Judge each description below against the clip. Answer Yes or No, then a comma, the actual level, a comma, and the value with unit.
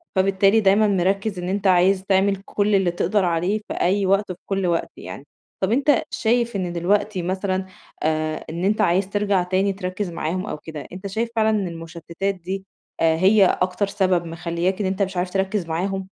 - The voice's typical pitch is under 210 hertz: Yes, high, 190 Hz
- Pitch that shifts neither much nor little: No, narrow, 2.2 semitones